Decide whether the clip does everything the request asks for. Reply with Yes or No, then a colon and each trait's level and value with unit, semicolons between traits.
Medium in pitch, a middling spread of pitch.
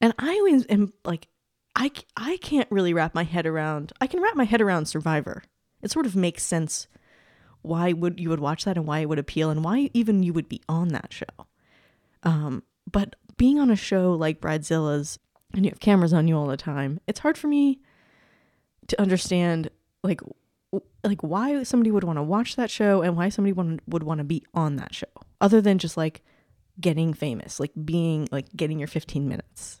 Yes: medium, 175 Hz; average, 5.0 semitones